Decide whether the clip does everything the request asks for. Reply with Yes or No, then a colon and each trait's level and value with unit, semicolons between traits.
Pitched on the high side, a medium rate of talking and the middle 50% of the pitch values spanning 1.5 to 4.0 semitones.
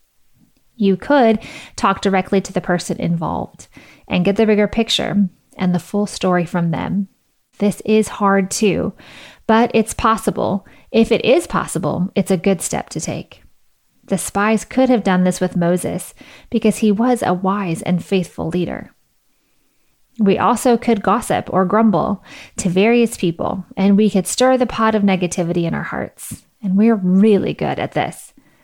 Yes: high, 200 Hz; average, 165 wpm; average, 3.3 semitones